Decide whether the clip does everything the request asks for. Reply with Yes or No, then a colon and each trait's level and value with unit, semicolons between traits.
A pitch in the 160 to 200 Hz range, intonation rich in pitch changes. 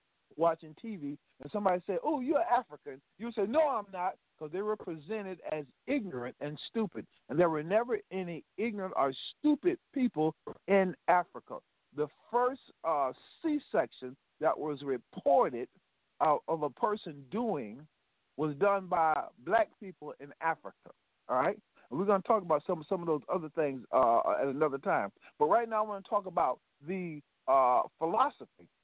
Yes: medium, 185 Hz; wide, 6.3 semitones